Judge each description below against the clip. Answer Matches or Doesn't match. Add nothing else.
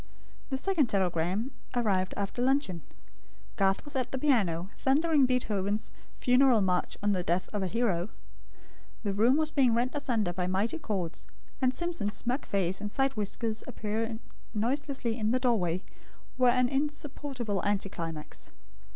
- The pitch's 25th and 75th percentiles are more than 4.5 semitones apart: Matches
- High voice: Matches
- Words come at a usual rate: Matches